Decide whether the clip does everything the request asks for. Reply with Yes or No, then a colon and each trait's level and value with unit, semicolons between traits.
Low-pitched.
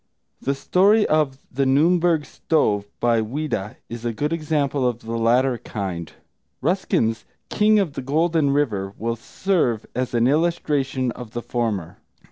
Yes: low, 130 Hz